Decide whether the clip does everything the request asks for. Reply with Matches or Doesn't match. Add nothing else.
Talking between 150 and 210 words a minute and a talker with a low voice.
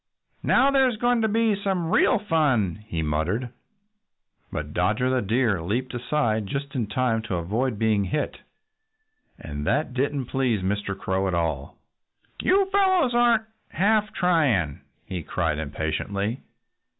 Doesn't match